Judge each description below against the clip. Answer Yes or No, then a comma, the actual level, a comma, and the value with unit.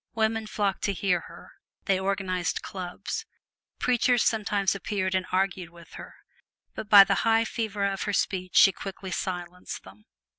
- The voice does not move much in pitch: Yes, narrow, 2.2 semitones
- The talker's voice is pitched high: Yes, high, 195 Hz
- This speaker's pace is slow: No, average, 155 wpm